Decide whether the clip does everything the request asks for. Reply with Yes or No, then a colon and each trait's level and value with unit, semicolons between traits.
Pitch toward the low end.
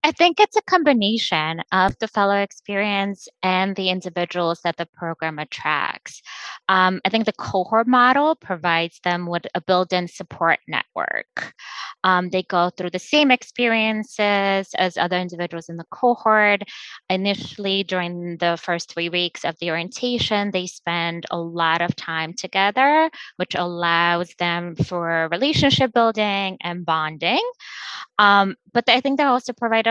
No: medium, 185 Hz